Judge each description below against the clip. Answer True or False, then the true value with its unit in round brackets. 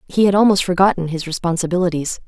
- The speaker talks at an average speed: True (160 wpm)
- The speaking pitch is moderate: True (180 Hz)